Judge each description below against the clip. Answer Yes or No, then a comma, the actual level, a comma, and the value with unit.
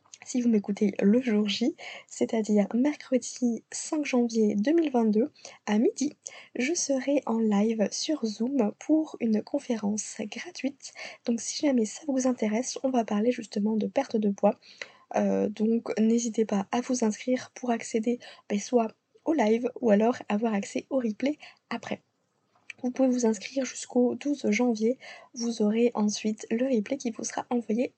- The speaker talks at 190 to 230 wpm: No, average, 155 wpm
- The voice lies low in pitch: No, high, 235 Hz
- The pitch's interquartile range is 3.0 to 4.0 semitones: Yes, average, 3.3 semitones